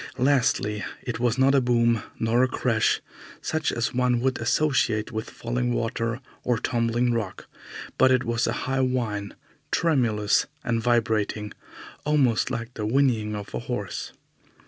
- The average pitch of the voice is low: Yes, low, 120 Hz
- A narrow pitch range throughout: Yes, narrow, 2.3 semitones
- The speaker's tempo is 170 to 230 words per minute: No, average, 145 wpm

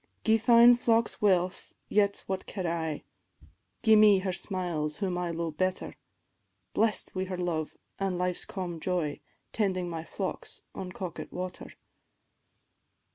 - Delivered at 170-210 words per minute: No, slow, 135 wpm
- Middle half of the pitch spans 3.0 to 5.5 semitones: No, narrow, 2.6 semitones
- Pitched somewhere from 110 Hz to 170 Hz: No, medium, 185 Hz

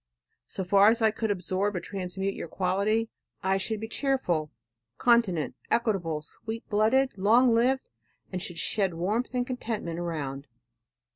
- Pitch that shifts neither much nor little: Yes, average, 4.1 semitones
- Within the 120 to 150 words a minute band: Yes, average, 145 wpm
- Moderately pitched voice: No, high, 200 Hz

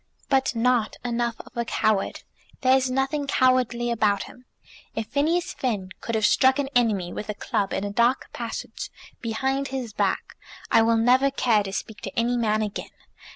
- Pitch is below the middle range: No, high, 235 Hz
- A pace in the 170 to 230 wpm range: Yes, average, 180 wpm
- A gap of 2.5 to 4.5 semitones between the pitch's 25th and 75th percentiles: Yes, average, 3.3 semitones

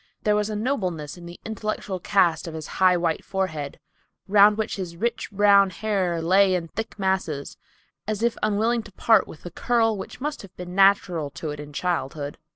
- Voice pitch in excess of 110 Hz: Yes, high, 190 Hz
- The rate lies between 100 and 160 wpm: No, average, 190 wpm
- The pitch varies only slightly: No, average, 3.8 semitones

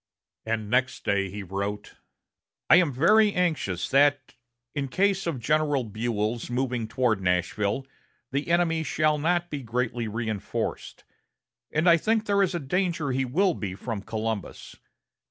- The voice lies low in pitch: Yes, low, 130 Hz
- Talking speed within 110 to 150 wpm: Yes, average, 140 wpm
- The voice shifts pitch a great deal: Yes, wide, 7.1 semitones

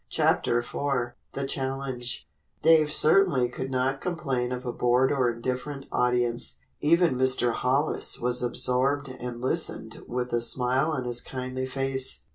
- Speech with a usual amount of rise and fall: No, narrow, 2.0 semitones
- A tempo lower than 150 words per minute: Yes, average, 140 wpm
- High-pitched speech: No, low, 130 Hz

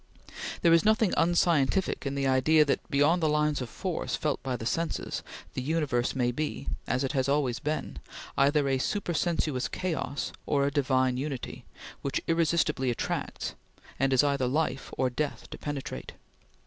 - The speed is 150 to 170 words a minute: Yes, average, 160 wpm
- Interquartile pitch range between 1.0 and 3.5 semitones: Yes, average, 3.2 semitones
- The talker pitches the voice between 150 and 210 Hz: No, medium, 140 Hz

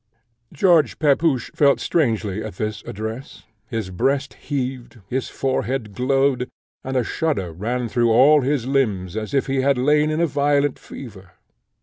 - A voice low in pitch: Yes, low, 130 Hz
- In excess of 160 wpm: No, average, 150 wpm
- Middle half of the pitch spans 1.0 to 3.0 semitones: No, average, 4.3 semitones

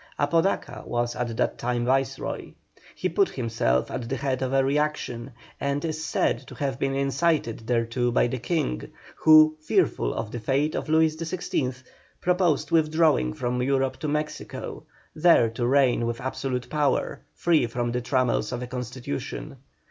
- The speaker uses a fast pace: No, average, 160 wpm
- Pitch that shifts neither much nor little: Yes, average, 4.0 semitones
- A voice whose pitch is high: No, low, 135 Hz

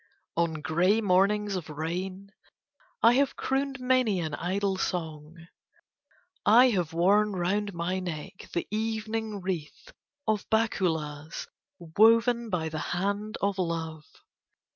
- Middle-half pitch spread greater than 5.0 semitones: No, average, 4.3 semitones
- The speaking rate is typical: No, slow, 120 wpm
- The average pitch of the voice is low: No, high, 190 Hz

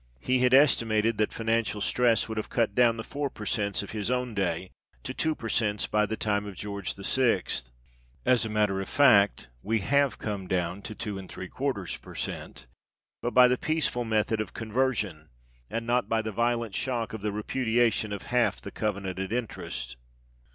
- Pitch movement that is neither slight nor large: Yes, average, 3.1 semitones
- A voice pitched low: Yes, low, 110 Hz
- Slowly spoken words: No, average, 180 wpm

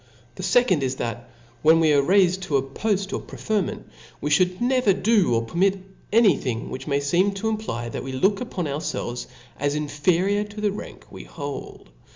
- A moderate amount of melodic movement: No, wide, 6.3 semitones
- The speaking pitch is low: No, medium, 175 Hz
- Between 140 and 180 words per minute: No, average, 195 wpm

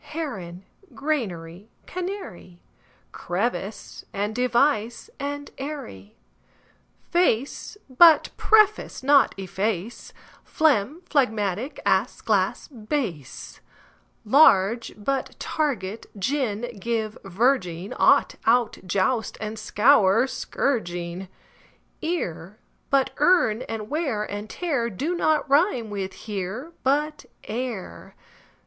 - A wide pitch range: Yes, wide, 6.4 semitones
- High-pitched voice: Yes, high, 230 Hz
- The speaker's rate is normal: No, slow, 95 wpm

